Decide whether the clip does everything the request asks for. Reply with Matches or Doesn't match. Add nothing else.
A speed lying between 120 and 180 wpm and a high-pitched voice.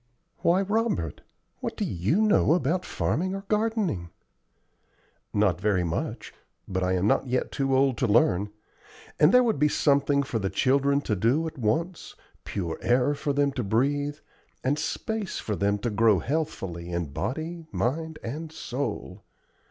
Doesn't match